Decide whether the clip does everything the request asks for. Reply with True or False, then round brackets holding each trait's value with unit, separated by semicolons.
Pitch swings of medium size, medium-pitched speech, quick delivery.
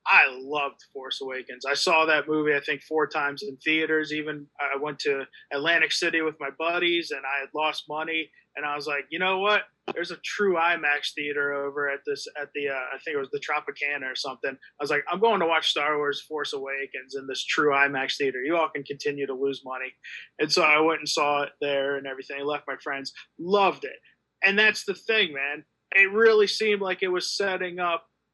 True (3.9 semitones; 150 Hz; 225 wpm)